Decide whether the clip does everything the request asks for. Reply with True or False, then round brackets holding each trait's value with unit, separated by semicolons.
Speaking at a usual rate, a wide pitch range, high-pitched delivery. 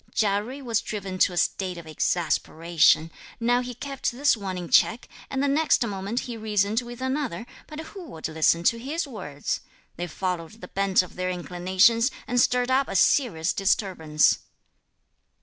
True (170 wpm; 5.7 semitones; 205 Hz)